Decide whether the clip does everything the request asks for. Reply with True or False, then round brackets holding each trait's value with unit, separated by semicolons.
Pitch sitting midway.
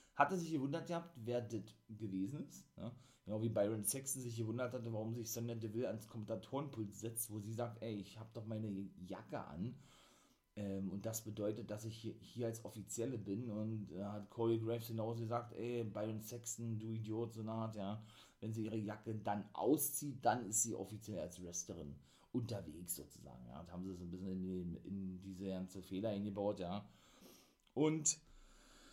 False (110 Hz)